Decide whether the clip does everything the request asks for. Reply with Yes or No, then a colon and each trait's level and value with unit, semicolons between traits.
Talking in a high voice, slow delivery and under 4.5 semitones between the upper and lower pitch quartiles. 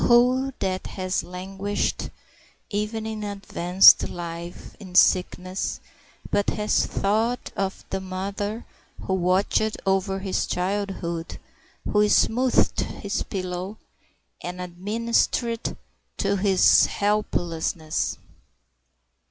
Yes: high, 195 Hz; slow, 95 wpm; narrow, 2.4 semitones